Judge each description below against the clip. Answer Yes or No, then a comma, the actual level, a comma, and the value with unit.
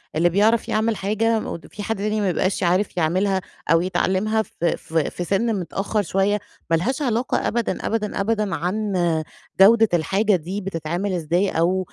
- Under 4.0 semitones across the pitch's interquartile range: Yes, average, 3.4 semitones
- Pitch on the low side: No, high, 195 Hz